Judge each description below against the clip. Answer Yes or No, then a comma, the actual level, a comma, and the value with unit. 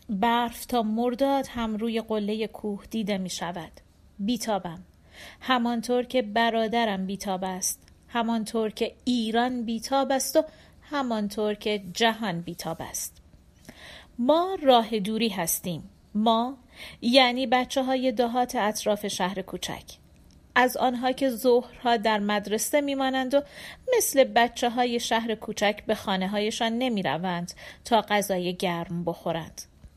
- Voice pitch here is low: No, high, 225 Hz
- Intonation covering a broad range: No, average, 4.2 semitones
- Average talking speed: Yes, average, 120 wpm